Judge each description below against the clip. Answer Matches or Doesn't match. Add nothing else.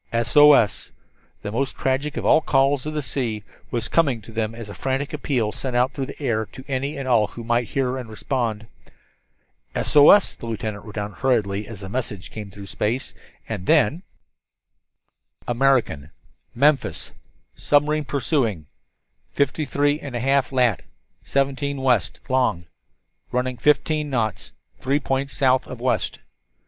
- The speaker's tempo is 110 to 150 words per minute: Matches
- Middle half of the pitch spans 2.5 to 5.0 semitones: Matches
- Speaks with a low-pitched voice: Matches